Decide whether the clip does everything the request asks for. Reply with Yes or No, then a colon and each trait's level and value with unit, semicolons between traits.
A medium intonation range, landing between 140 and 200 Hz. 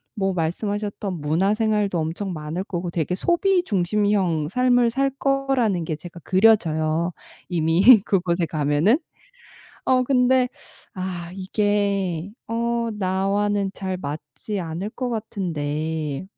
Yes: average, 4.4 semitones; high, 190 Hz